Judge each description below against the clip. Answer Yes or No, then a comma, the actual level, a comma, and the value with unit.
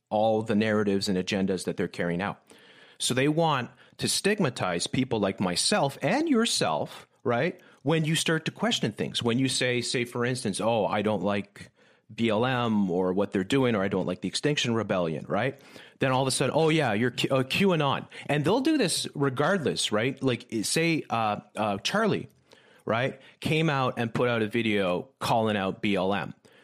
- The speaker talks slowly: No, average, 185 wpm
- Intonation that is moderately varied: No, wide, 6.0 semitones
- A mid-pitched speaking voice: No, low, 125 Hz